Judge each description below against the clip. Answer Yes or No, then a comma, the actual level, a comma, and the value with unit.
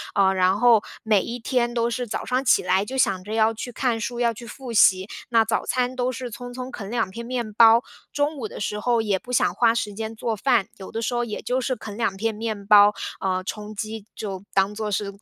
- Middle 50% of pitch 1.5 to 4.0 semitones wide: Yes, average, 2.8 semitones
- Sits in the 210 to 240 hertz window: Yes, high, 225 Hz